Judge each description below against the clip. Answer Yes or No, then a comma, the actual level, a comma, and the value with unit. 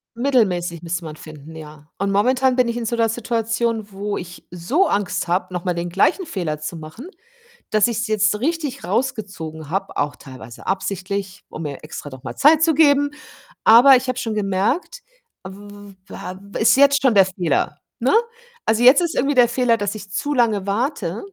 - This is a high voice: Yes, high, 205 Hz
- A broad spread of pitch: Yes, wide, 6.0 semitones